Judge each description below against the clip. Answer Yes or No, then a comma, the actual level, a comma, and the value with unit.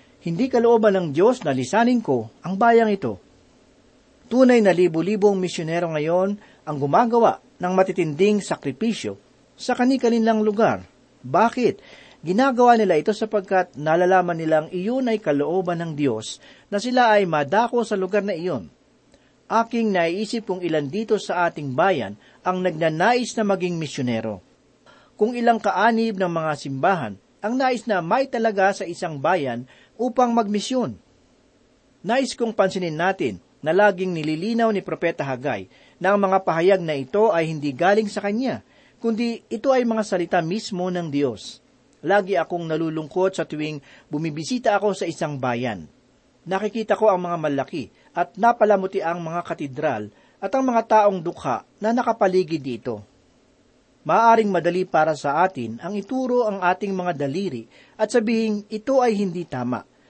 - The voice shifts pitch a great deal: Yes, wide, 5.9 semitones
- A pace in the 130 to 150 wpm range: Yes, average, 145 wpm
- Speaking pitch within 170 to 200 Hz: Yes, high, 190 Hz